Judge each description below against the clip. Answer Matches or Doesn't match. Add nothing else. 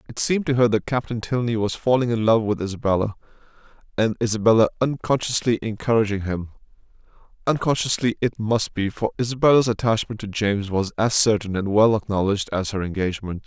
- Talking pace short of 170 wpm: Matches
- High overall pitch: Doesn't match